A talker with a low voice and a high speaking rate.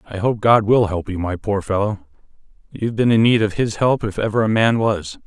Yes: low, 105 Hz; fast, 230 wpm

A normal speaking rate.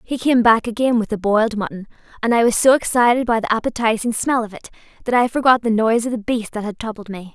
No: fast, 255 wpm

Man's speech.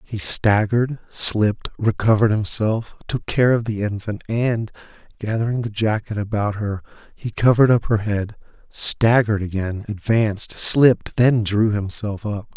Yes: male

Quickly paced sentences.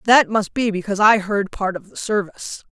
Yes: fast, 220 wpm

